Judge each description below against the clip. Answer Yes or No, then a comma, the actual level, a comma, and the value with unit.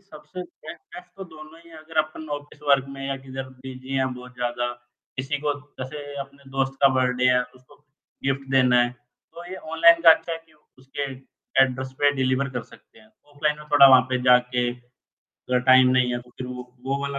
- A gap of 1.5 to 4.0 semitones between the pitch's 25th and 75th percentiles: Yes, average, 2.8 semitones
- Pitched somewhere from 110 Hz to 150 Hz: Yes, low, 135 Hz